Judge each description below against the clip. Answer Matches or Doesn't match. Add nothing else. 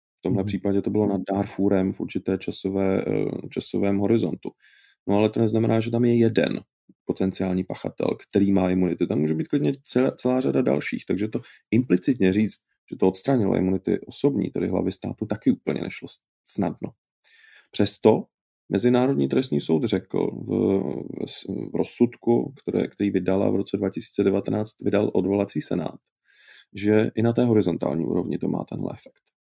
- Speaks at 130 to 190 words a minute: Matches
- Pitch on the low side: Matches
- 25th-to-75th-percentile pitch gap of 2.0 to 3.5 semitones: Matches